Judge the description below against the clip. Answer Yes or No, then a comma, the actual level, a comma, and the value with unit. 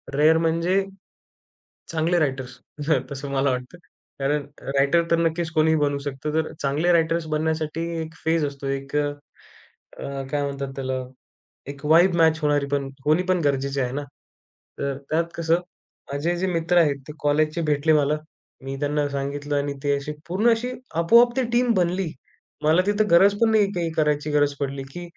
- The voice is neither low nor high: Yes, medium, 155 Hz